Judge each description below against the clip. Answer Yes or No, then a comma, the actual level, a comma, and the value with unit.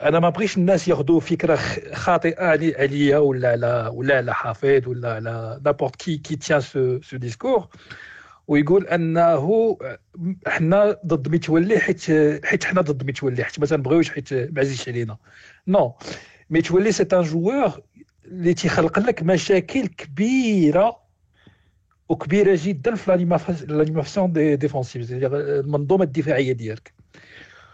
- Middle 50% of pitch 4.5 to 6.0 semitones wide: Yes, average, 5.1 semitones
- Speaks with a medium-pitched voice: Yes, medium, 155 Hz